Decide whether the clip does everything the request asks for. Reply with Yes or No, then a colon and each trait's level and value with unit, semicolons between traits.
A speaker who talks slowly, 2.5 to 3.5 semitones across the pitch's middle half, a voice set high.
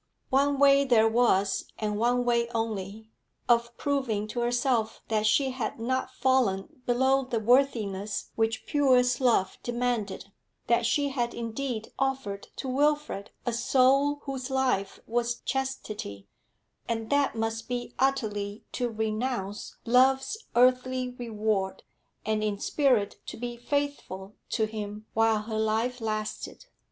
Yes: slow, 130 wpm; average, 3.2 semitones; high, 235 Hz